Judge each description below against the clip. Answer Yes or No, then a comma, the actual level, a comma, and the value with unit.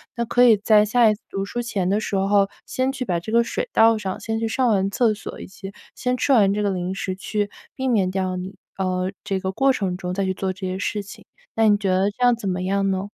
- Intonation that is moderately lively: Yes, average, 3.0 semitones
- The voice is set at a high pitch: Yes, high, 200 Hz